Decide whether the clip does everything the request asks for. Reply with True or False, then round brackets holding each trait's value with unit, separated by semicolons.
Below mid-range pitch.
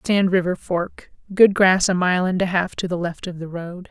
False (180 Hz)